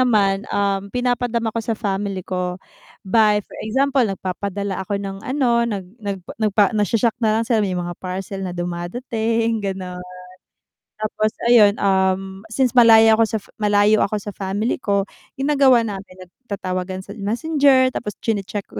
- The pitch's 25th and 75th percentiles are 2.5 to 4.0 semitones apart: Yes, average, 3.0 semitones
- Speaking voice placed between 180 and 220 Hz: Yes, high, 210 Hz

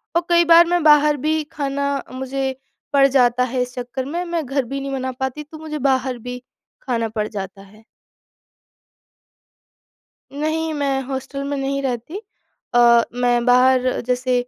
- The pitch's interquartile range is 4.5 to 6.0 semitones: No, average, 2.8 semitones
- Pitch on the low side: No, very high, 265 Hz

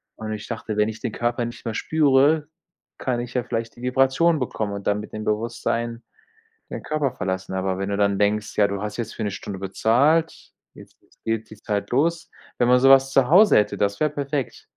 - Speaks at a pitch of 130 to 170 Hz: No, low, 115 Hz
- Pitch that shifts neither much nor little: Yes, average, 4.5 semitones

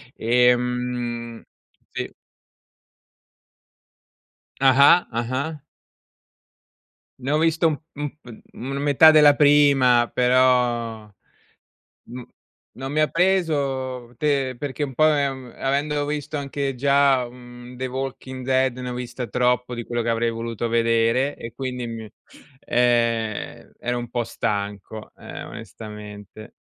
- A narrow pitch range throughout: No, average, 3.0 semitones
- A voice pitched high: No, low, 125 Hz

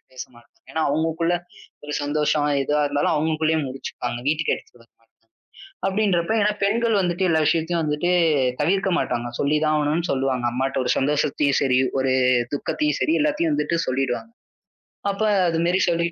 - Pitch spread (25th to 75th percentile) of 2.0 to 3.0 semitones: No, average, 3.9 semitones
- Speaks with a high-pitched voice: No, medium, 155 Hz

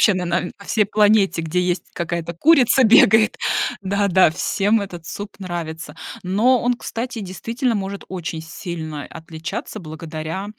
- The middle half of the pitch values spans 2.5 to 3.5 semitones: No, average, 4.2 semitones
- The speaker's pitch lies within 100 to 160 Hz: No, medium, 185 Hz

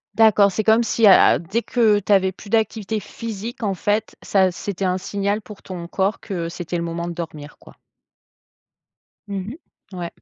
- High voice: Yes, high, 200 Hz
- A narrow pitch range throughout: No, average, 3.2 semitones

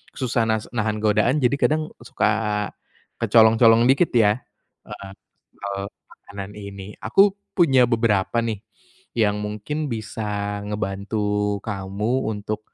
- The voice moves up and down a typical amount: No, narrow, 2.3 semitones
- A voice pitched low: Yes, low, 105 Hz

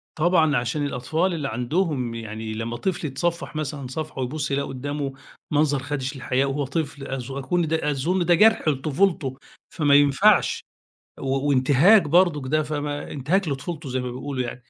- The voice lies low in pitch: No, medium, 145 Hz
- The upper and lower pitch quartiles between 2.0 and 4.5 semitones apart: Yes, average, 3.3 semitones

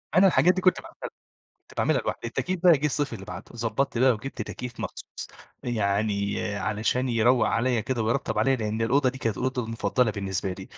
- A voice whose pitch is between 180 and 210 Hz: No, low, 120 Hz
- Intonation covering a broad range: No, average, 3.8 semitones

